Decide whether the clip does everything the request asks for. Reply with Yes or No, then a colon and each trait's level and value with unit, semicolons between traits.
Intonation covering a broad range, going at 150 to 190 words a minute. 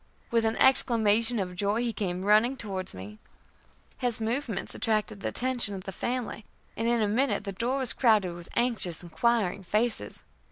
No: average, 3.5 semitones; average, 170 wpm